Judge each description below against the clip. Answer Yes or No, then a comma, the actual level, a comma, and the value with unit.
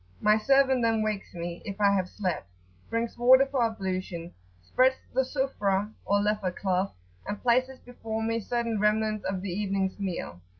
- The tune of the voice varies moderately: Yes, average, 3.6 semitones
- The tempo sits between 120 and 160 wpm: No, average, 170 wpm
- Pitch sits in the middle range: No, high, 210 Hz